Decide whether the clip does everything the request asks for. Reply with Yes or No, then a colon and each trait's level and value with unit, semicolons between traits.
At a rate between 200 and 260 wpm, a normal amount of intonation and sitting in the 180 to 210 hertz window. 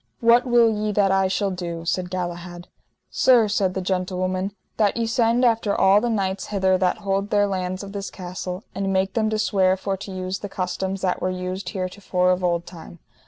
No: fast, 205 wpm; narrow, 2.0 semitones; high, 190 Hz